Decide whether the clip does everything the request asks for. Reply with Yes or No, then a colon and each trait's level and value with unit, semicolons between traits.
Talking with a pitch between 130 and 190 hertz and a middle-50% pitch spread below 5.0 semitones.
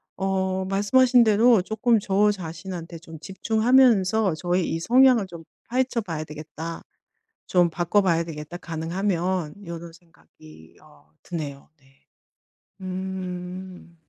Yes: medium, 185 Hz; average, 3.7 semitones